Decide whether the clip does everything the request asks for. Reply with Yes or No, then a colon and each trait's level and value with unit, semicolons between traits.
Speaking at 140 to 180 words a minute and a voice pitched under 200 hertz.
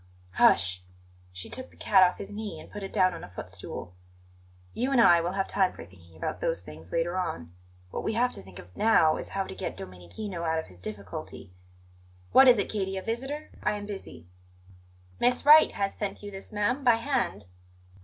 No: fast, 205 wpm; high, 190 Hz